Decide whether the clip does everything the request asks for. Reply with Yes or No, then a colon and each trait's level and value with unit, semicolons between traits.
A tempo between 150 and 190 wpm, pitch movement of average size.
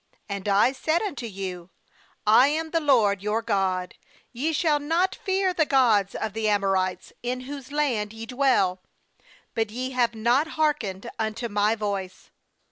No: average, 155 wpm; wide, 6.0 semitones